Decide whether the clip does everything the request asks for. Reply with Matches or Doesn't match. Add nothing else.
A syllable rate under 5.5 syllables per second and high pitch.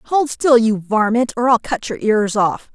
Matches